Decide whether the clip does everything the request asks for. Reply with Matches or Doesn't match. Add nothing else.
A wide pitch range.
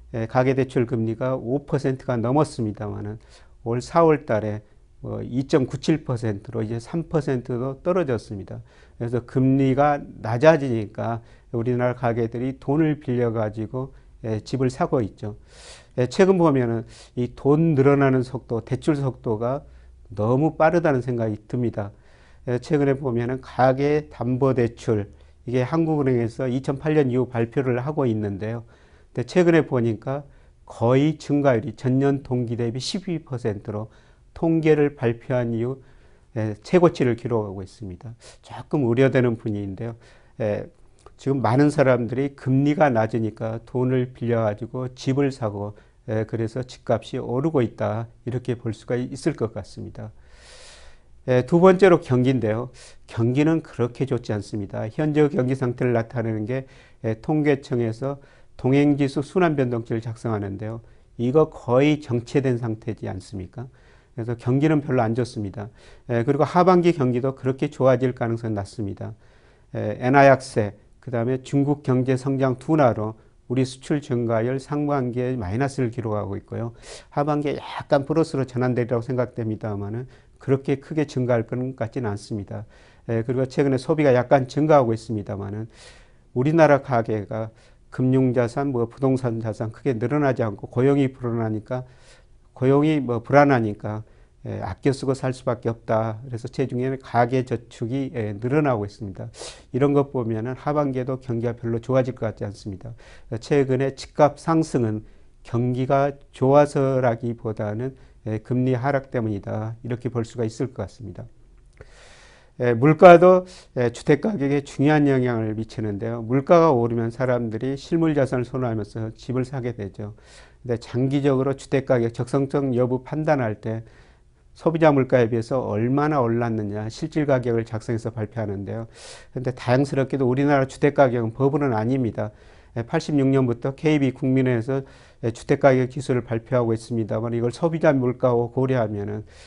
Doesn't match